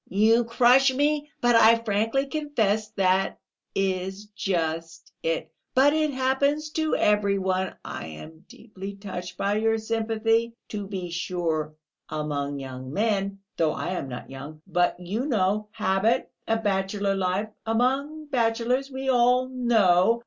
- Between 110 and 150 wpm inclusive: Yes, average, 140 wpm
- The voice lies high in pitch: Yes, high, 210 Hz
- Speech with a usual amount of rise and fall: Yes, average, 4.8 semitones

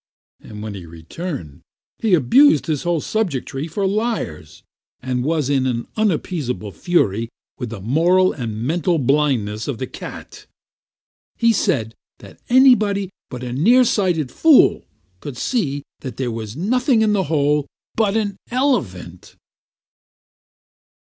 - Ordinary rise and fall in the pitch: No, wide, 8.9 semitones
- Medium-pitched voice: Yes, medium, 150 Hz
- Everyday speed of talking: No, slow, 130 wpm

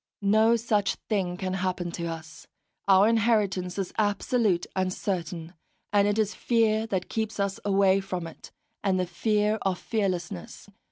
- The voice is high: Yes, high, 195 Hz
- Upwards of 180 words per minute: No, average, 155 wpm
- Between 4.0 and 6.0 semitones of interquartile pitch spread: No, average, 2.9 semitones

